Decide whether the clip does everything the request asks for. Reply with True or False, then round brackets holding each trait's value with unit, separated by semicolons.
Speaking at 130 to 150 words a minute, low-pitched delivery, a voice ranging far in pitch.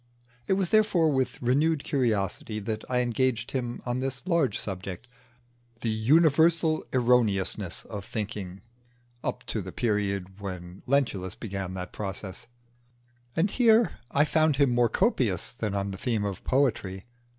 True (140 wpm; 120 Hz; 6.1 semitones)